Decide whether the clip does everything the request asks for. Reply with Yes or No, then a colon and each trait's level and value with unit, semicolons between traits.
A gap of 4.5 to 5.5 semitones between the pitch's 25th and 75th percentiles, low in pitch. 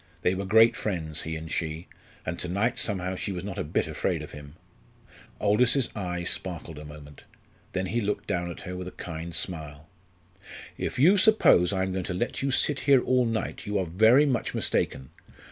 Yes: average, 5.2 semitones; very low, 95 Hz